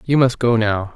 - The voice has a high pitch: No, low, 115 Hz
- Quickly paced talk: Yes, fast, 255 wpm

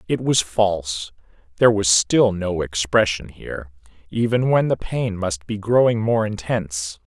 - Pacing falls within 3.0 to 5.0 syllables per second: Yes, 4.5 syllables/s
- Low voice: Yes, low, 100 Hz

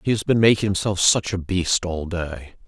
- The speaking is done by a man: Yes, male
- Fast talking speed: Yes, fast, 225 wpm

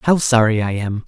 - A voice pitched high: No, low, 115 Hz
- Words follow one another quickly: Yes, fast, 225 wpm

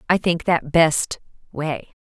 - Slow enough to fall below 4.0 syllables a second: Yes, 3.5 syllables/s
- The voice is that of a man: No, female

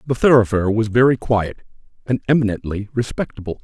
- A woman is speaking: No, male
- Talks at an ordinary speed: No, slow, 130 wpm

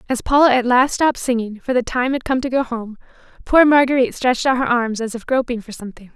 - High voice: Yes, high, 245 Hz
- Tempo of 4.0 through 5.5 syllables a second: No, 6.4 syllables/s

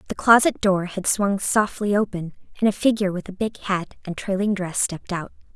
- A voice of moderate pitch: No, high, 195 Hz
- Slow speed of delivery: No, fast, 205 wpm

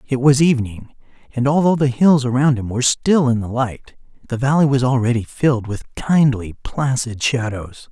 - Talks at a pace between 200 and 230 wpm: No, average, 175 wpm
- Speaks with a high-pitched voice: No, low, 130 Hz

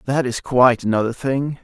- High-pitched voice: No, low, 125 Hz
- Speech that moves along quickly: No, average, 185 wpm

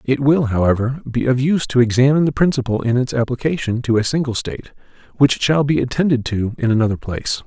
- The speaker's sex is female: No, male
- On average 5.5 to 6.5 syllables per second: Yes, 6.3 syllables/s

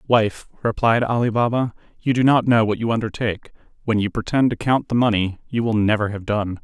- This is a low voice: Yes, low, 115 Hz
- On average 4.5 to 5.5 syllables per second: No, 5.7 syllables/s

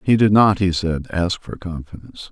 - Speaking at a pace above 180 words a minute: Yes, fast, 205 wpm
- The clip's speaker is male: Yes, male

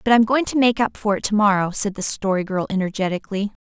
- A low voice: No, high, 205 Hz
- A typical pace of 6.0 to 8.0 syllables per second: Yes, 6.3 syllables/s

